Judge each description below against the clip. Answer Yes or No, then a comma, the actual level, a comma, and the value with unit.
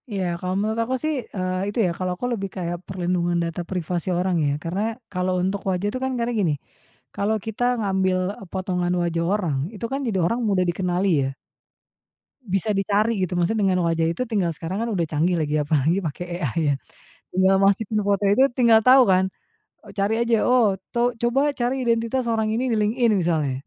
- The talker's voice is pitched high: Yes, high, 195 Hz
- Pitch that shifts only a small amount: No, average, 4.1 semitones